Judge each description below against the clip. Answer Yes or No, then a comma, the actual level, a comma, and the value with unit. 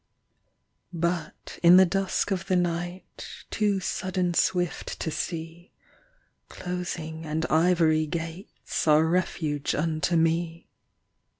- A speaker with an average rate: No, slow, 105 wpm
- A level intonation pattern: Yes, narrow, 2.1 semitones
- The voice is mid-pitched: Yes, medium, 170 Hz